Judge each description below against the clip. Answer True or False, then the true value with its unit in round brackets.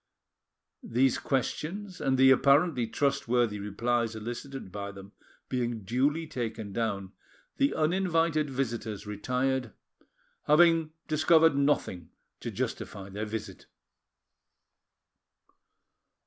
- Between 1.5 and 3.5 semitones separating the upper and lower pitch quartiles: False (5.6 semitones)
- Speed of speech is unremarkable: False (90 wpm)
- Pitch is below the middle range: True (125 Hz)